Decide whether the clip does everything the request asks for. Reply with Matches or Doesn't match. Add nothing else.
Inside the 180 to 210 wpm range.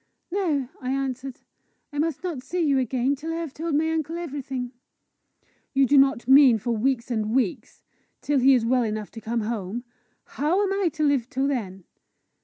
Matches